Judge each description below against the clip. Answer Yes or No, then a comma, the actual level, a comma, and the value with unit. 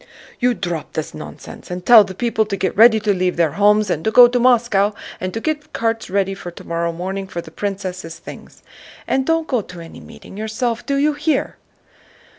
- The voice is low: No, high, 205 Hz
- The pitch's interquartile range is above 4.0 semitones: Yes, average, 4.9 semitones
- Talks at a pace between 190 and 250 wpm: Yes, average, 200 wpm